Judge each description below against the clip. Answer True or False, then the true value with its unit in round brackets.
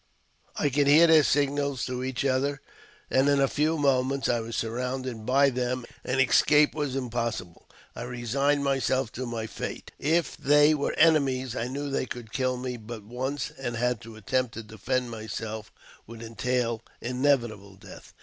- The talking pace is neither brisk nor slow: True (165 wpm)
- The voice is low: True (130 Hz)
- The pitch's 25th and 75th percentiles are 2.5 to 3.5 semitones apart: True (3.1 semitones)